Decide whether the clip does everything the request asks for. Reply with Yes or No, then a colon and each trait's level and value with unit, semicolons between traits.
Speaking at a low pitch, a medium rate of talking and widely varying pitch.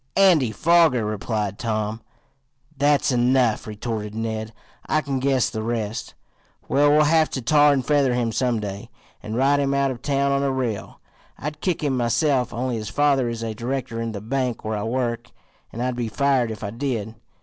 No: low, 125 Hz; average, 185 wpm; average, 3.8 semitones